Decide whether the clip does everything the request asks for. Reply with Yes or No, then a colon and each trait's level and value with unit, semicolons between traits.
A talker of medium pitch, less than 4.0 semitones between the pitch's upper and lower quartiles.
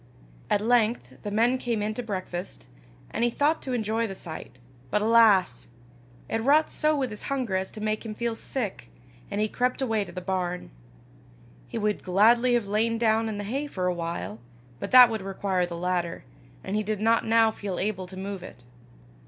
No: high, 215 Hz; average, 3.6 semitones